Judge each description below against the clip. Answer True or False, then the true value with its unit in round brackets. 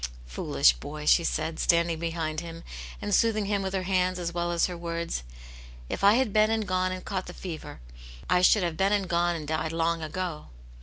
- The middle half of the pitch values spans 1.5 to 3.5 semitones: True (2.5 semitones)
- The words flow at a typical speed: False (210 wpm)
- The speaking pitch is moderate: True (175 Hz)